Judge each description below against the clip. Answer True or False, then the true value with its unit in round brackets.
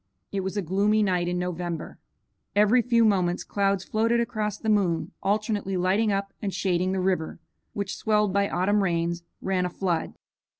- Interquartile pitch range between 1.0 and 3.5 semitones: True (2.7 semitones)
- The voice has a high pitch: True (195 Hz)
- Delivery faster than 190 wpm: False (170 wpm)